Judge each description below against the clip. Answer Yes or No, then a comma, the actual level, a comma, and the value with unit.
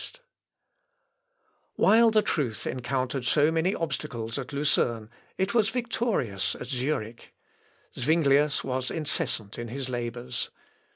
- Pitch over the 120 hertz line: Yes, low, 135 Hz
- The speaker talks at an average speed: No, slow, 115 wpm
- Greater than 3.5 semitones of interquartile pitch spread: Yes, average, 5.2 semitones